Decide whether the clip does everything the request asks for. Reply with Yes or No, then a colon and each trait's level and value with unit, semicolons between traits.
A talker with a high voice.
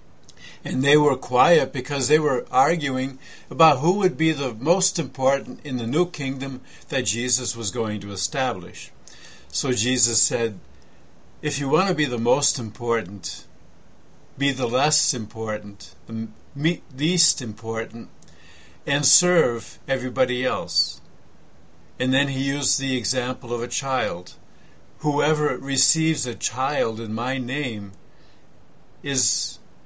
No: low, 130 Hz